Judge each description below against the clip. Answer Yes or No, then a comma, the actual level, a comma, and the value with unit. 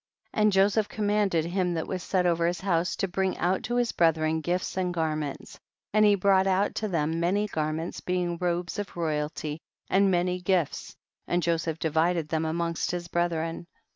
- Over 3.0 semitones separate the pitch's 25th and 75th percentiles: No, average, 2.7 semitones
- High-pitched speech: No, medium, 175 Hz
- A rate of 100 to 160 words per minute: No, average, 185 wpm